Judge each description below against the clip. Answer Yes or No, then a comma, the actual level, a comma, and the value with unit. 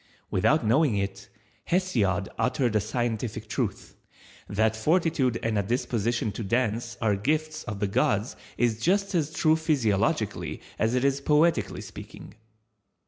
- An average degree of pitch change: No, wide, 6.2 semitones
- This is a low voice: Yes, low, 120 Hz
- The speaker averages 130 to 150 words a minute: Yes, average, 140 wpm